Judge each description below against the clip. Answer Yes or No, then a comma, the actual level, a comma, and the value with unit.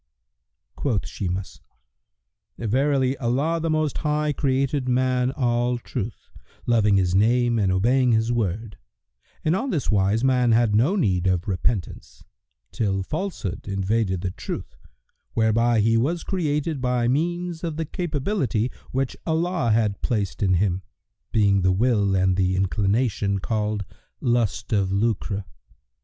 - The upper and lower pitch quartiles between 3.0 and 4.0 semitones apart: No, wide, 5.4 semitones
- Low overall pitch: Yes, low, 115 Hz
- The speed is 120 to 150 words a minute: Yes, slow, 135 wpm